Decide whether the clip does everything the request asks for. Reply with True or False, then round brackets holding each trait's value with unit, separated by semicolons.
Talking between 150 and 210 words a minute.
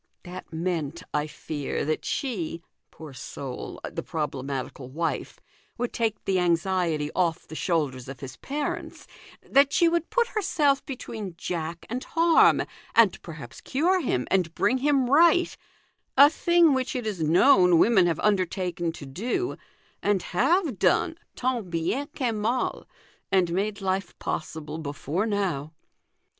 False (140 wpm)